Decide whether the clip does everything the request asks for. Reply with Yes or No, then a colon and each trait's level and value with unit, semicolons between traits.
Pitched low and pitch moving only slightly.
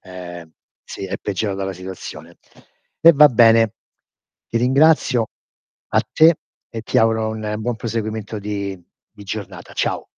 No: low, 110 Hz; average, 3.2 semitones